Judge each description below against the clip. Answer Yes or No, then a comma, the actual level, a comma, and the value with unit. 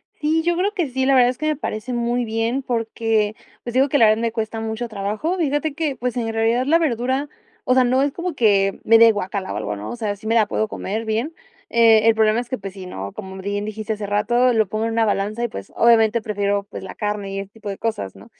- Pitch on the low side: No, high, 225 Hz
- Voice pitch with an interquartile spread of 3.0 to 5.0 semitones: Yes, average, 3.3 semitones